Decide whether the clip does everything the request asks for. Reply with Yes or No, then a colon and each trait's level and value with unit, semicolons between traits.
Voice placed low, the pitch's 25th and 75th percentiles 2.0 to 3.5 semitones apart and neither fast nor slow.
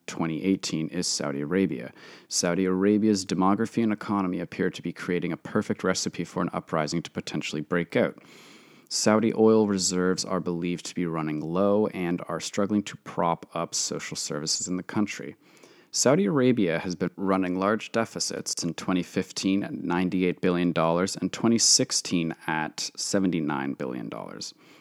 Yes: very low, 90 Hz; average, 2.9 semitones; average, 145 wpm